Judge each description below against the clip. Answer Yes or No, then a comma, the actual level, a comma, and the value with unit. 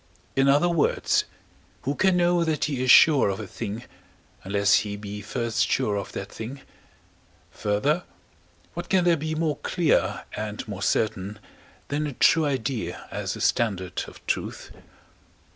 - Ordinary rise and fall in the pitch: No, wide, 6.9 semitones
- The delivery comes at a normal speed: Yes, average, 155 wpm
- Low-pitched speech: Yes, low, 125 Hz